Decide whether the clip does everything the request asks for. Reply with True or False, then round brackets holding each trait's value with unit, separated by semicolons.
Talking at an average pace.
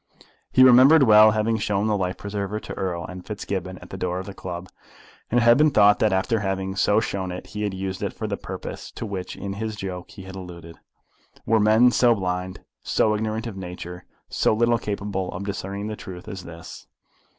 False (210 wpm)